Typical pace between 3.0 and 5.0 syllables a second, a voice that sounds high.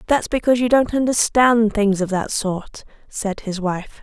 Yes: 4.4 syllables/s; high, 220 Hz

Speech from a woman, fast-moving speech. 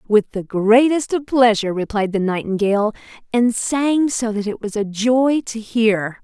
No: female; average, 175 wpm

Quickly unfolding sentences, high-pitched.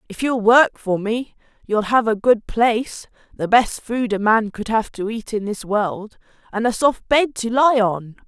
Yes: fast, 210 wpm; high, 225 Hz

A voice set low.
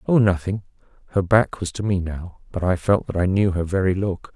Yes: very low, 95 Hz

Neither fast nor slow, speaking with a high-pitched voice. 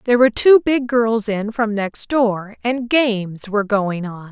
Yes: average, 195 wpm; high, 225 Hz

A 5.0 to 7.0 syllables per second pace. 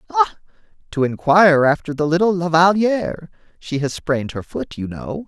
Yes: 5.1 syllables/s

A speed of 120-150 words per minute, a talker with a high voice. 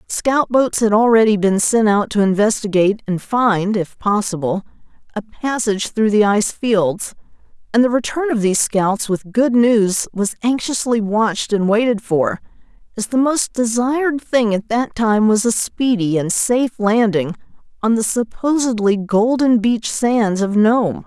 No: average, 160 wpm; high, 220 Hz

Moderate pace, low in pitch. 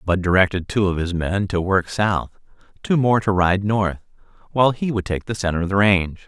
No: fast, 220 wpm; very low, 95 Hz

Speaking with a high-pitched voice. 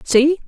Yes: very high, 300 Hz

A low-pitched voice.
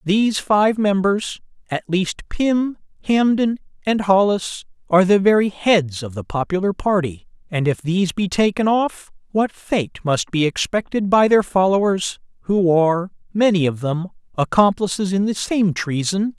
No: high, 195 Hz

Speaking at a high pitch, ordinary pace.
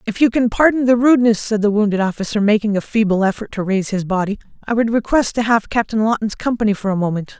No: high, 215 Hz; fast, 235 wpm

